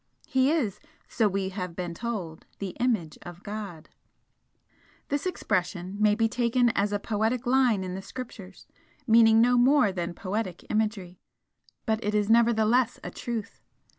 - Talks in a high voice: Yes, high, 215 Hz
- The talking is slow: No, average, 150 wpm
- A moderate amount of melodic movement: Yes, average, 3.9 semitones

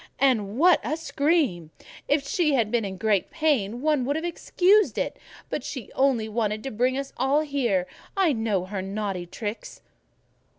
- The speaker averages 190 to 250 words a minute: No, average, 170 wpm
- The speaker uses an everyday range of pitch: No, wide, 5.9 semitones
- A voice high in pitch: Yes, very high, 250 Hz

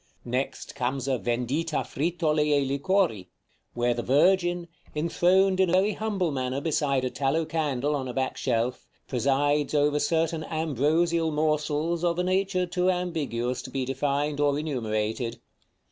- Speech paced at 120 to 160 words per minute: Yes, average, 145 wpm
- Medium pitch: Yes, medium, 150 Hz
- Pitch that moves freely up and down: No, average, 4.4 semitones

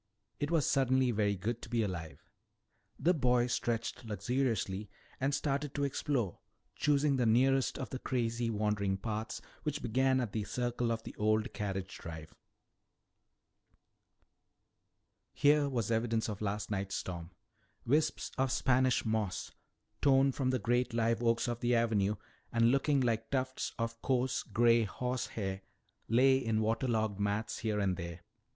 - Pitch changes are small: No, average, 3.5 semitones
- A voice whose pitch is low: Yes, low, 115 Hz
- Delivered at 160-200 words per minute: No, average, 145 wpm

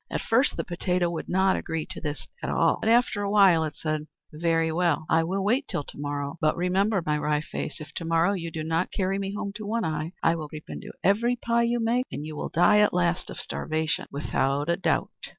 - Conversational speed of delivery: No, fast, 240 wpm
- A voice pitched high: No, medium, 170 Hz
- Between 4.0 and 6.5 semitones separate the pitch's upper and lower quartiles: Yes, average, 4.3 semitones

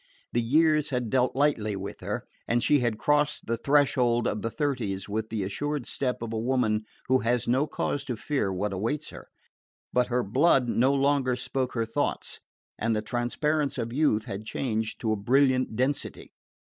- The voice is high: No, low, 125 Hz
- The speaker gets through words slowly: No, average, 185 wpm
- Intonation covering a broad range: No, average, 3.9 semitones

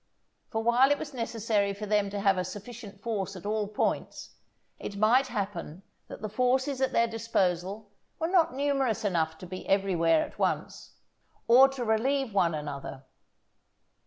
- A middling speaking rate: Yes, average, 160 wpm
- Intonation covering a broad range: No, average, 4.3 semitones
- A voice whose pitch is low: No, high, 215 Hz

